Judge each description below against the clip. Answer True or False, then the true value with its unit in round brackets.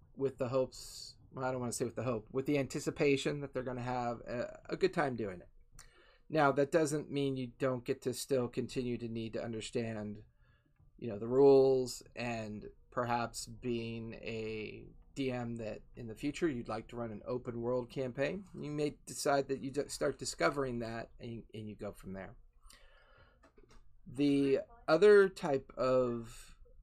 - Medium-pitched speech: False (125 Hz)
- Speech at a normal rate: True (170 wpm)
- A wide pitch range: False (3.1 semitones)